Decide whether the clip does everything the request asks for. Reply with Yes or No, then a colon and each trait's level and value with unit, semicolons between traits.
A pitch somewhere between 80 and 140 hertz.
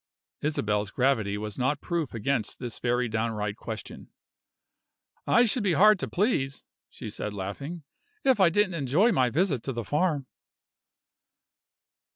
Yes: low, 135 Hz